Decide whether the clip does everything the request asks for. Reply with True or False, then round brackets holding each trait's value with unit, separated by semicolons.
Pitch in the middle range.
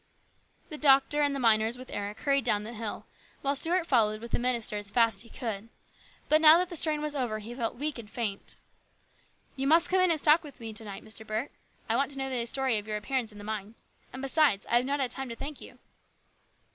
False (250 Hz)